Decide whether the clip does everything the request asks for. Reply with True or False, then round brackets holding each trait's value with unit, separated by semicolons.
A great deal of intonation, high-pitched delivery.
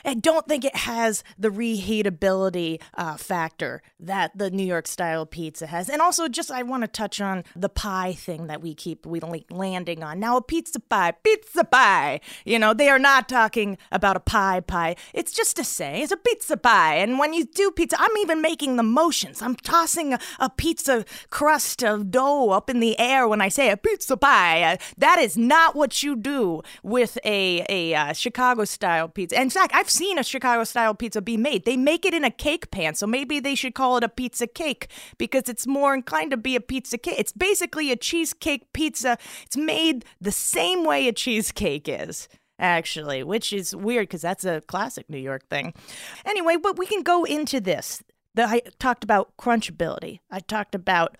True (7.3 semitones; 240 Hz)